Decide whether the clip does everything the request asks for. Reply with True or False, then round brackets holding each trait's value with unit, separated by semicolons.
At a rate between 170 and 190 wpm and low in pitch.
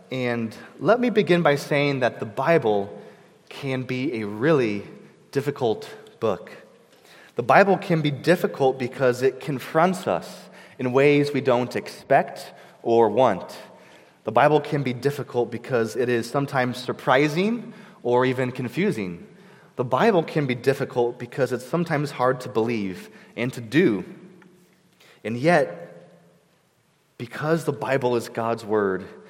False (135 wpm; 130 Hz)